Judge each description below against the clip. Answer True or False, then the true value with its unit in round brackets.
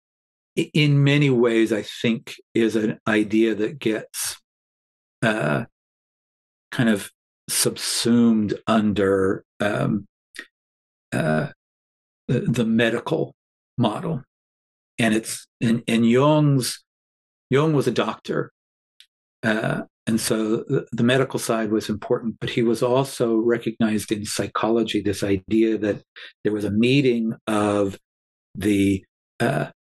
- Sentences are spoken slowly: True (110 wpm)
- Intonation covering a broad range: False (3.0 semitones)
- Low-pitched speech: True (110 Hz)